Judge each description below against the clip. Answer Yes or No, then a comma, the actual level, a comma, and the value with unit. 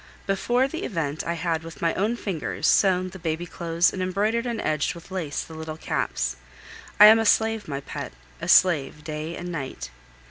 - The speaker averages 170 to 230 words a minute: Yes, average, 190 wpm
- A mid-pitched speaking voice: Yes, medium, 170 Hz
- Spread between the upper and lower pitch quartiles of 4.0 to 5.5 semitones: Yes, average, 4.3 semitones